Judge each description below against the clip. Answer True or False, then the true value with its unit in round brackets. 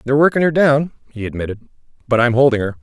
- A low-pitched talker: True (130 Hz)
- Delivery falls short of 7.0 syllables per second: False (7.4 syllables/s)